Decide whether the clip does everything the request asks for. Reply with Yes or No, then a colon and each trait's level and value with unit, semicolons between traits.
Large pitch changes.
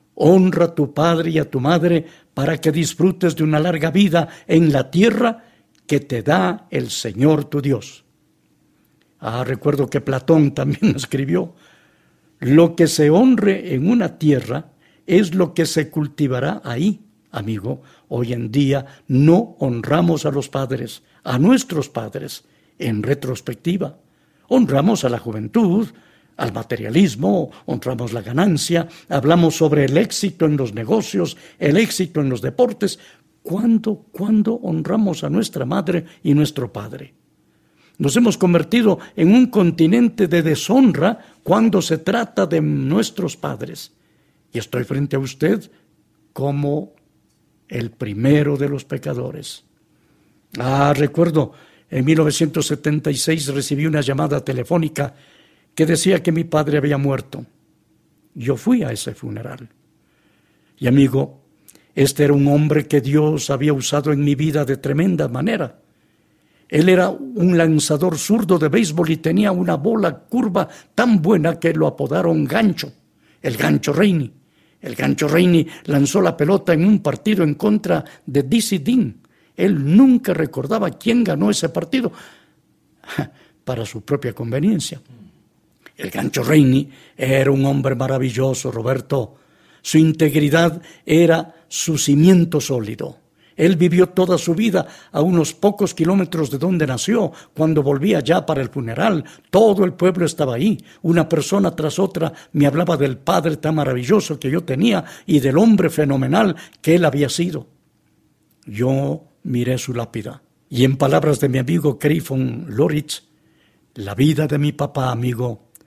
No: average, 4.3 semitones